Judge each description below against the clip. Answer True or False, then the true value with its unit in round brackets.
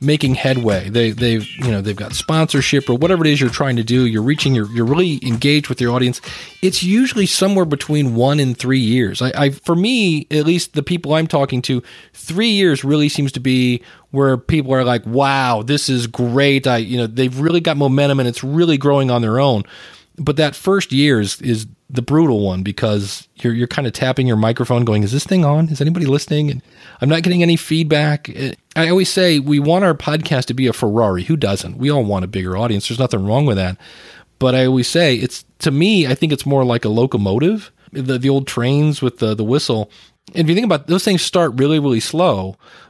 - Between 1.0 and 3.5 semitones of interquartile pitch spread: False (4.5 semitones)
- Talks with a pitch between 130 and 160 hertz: True (135 Hz)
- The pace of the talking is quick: True (230 wpm)